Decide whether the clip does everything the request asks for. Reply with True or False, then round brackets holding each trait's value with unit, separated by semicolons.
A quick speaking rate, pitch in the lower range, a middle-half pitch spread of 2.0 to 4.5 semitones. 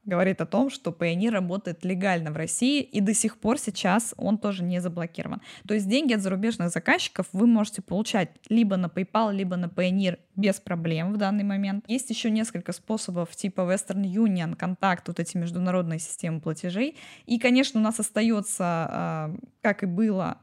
False (175 wpm; 195 Hz; 3.5 semitones)